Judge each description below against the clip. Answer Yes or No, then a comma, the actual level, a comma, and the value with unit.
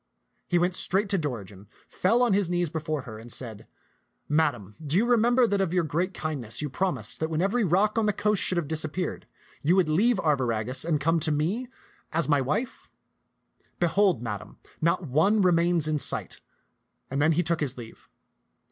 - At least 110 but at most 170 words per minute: No, average, 190 wpm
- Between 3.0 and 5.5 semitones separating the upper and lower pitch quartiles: Yes, average, 4.8 semitones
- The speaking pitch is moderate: Yes, medium, 165 Hz